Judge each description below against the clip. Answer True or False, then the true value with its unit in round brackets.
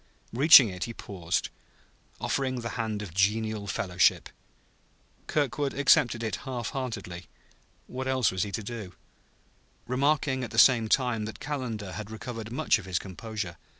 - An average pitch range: True (3.9 semitones)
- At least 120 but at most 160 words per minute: True (150 wpm)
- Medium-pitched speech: False (115 Hz)